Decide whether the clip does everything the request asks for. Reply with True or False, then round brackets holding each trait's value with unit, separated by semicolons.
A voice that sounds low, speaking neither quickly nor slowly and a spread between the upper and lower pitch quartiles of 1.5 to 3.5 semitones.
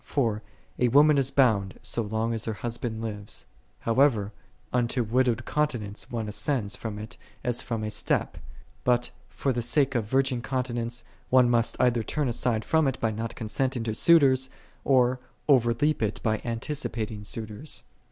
True (120 Hz; 170 wpm; 3.0 semitones)